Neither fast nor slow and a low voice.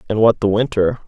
No: fast, 225 wpm; low, 110 Hz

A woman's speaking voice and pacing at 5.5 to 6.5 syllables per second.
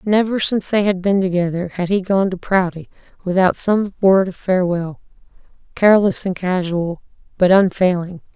No: female; 5.1 syllables/s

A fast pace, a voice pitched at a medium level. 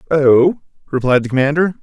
No: slow, 130 wpm; medium, 145 Hz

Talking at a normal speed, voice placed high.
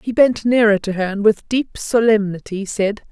Yes: average, 190 wpm; high, 215 Hz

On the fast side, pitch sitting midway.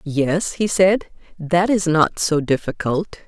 No: average, 145 wpm; medium, 170 Hz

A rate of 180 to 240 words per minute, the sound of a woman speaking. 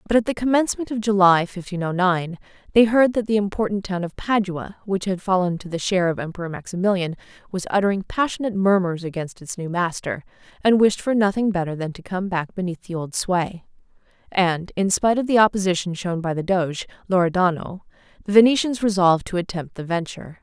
Yes: average, 190 wpm; female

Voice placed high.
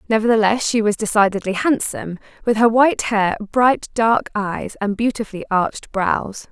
Yes: high, 215 Hz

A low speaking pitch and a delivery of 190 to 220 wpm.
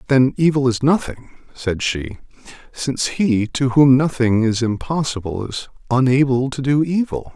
No: low, 130 Hz; average, 145 wpm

